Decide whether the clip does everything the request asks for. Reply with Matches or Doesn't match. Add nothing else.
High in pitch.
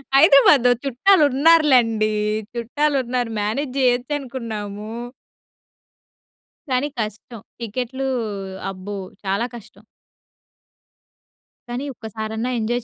Matches